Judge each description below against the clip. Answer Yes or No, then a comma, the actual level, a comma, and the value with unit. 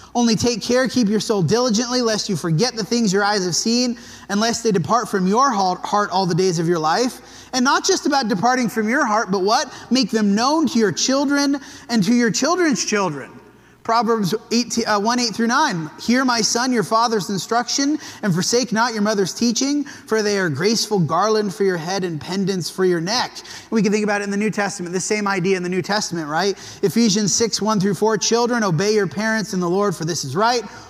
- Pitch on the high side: Yes, high, 215 Hz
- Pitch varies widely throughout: No, average, 3.4 semitones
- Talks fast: Yes, fast, 225 wpm